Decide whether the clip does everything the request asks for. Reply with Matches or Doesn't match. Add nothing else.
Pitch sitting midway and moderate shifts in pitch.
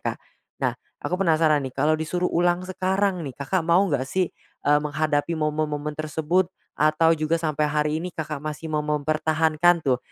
Doesn't match